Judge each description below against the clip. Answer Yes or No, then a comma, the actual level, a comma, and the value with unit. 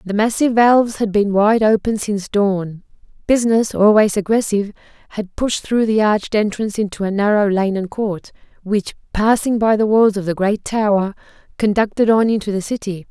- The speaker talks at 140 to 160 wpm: No, average, 175 wpm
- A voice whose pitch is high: Yes, high, 210 Hz